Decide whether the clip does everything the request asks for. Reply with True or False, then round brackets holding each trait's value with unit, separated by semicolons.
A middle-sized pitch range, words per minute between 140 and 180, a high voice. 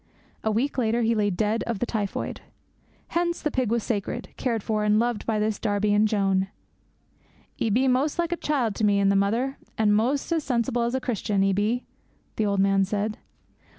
False (3.1 semitones; 205 wpm; 220 Hz)